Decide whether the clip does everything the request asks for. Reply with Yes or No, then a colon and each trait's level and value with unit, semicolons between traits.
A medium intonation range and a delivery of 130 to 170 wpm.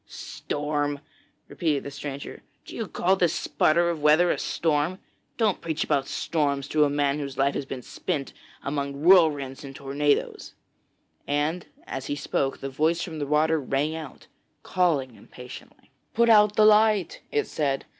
Yes: average, 3.3 semitones; average, 160 wpm